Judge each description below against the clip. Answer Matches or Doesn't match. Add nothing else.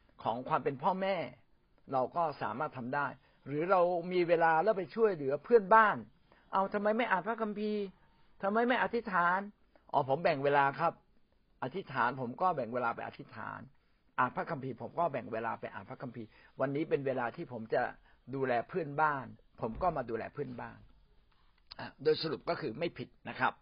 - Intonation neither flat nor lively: Doesn't match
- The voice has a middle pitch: Matches